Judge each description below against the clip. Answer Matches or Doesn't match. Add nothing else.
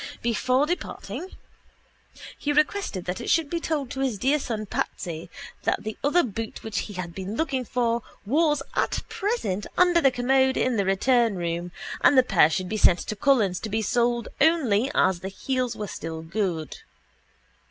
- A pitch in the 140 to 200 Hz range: Doesn't match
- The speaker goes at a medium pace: Matches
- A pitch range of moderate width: Doesn't match